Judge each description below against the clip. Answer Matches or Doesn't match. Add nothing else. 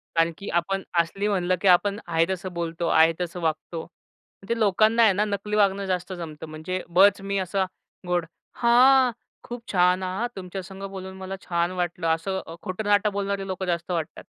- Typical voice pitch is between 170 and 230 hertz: Matches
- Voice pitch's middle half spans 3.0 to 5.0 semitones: Doesn't match